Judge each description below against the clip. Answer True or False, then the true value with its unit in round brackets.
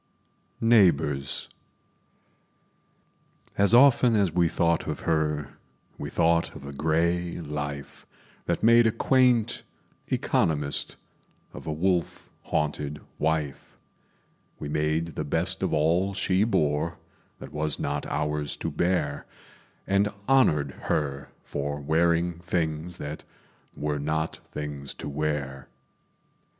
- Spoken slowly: True (115 wpm)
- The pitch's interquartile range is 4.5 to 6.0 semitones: False (3.2 semitones)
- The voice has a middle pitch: False (80 Hz)